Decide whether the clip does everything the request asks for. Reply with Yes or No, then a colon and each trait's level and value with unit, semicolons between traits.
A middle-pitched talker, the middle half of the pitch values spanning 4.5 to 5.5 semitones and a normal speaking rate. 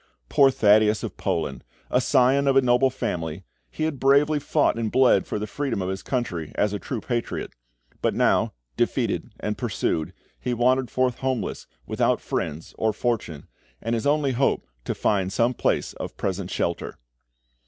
No: low, 120 Hz; average, 5.1 semitones; average, 170 wpm